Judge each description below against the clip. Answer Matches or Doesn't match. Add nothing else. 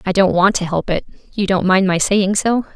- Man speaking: Doesn't match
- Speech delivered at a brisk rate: Matches